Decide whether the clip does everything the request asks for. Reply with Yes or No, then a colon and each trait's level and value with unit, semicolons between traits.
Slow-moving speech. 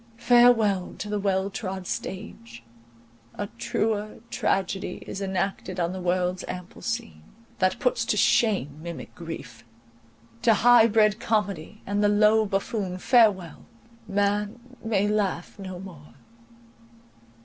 Yes: slow, 120 wpm